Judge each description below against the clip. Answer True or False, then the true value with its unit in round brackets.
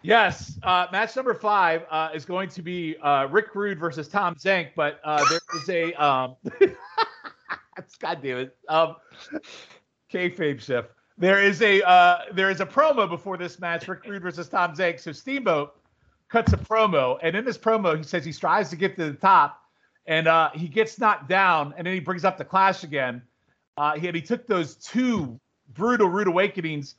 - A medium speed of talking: True (190 wpm)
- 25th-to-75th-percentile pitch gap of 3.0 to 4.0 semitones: False (4.4 semitones)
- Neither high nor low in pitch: True (180 Hz)